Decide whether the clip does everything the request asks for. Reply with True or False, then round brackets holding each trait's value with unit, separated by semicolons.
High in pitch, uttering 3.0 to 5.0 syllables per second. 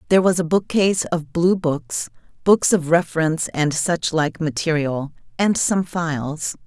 False (160 Hz; 4.8 syllables/s)